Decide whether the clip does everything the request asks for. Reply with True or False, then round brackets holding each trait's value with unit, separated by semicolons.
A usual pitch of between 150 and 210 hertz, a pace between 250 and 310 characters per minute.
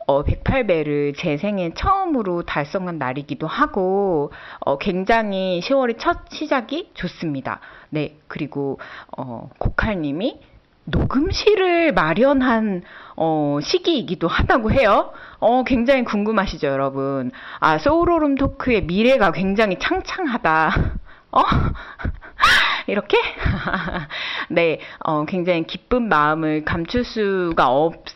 False (190 Hz; 240 characters per minute)